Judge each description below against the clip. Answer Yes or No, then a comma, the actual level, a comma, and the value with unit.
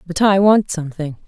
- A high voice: No, medium, 180 Hz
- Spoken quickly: No, average, 190 wpm